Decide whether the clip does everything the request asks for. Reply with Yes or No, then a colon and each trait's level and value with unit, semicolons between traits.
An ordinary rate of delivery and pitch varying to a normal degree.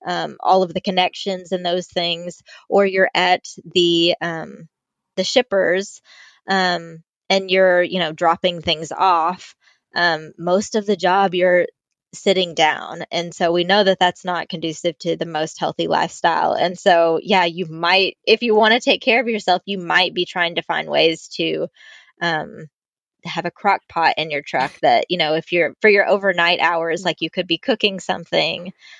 No: average, 180 wpm; narrow, 2.2 semitones